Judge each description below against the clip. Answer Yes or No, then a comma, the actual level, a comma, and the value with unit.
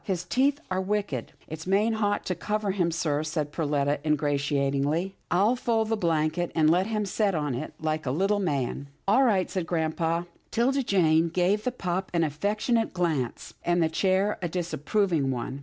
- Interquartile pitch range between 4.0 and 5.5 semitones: Yes, average, 4.9 semitones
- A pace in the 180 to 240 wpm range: Yes, average, 190 wpm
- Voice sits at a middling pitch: Yes, medium, 175 Hz